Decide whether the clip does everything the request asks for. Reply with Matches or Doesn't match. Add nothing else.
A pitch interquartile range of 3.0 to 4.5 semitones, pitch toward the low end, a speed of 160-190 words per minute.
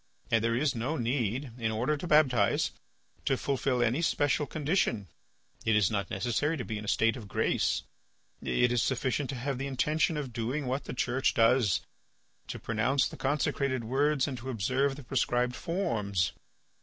Matches